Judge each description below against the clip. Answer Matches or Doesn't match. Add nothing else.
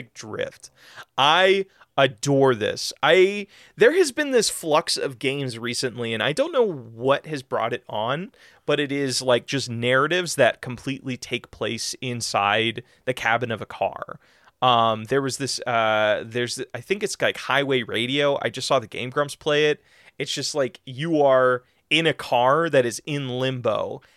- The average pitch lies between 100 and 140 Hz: Matches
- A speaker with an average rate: Matches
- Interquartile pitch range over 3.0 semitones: Matches